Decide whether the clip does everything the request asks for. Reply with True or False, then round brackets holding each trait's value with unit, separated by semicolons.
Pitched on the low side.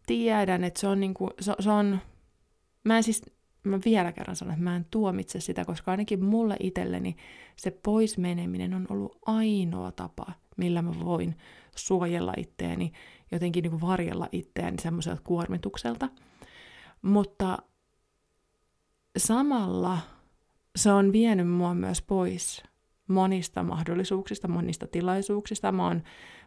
False (185 Hz)